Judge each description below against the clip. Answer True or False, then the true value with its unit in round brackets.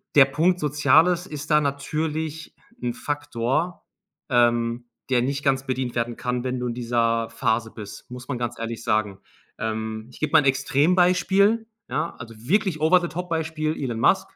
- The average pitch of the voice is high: False (135 Hz)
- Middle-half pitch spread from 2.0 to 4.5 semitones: False (5.1 semitones)